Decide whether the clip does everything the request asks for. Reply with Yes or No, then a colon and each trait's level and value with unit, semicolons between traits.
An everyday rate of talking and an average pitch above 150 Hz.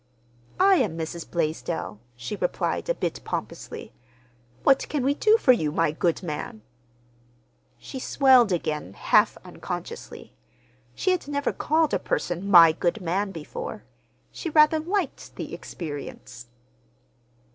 No: slow, 130 wpm; medium, 185 Hz